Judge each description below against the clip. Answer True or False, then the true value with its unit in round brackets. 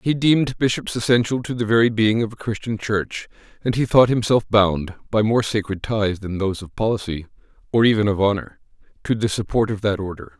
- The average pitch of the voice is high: False (110 Hz)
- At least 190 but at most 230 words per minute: True (200 wpm)